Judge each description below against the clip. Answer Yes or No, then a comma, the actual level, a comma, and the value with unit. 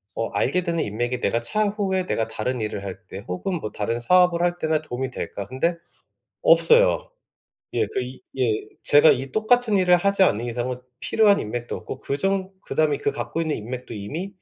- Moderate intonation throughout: No, wide, 7.9 semitones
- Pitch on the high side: No, medium, 145 Hz